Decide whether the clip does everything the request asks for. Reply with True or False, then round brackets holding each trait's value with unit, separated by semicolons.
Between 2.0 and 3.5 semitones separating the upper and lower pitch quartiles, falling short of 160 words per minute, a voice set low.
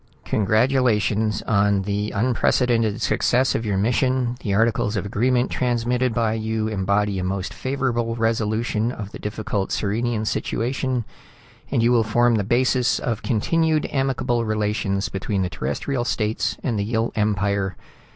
True (2.9 semitones; 140 wpm; 110 Hz)